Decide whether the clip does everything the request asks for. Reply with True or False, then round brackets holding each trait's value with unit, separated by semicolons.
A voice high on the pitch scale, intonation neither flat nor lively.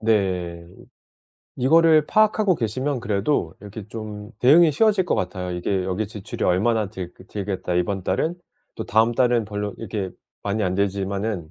False (105 Hz; 4.6 semitones)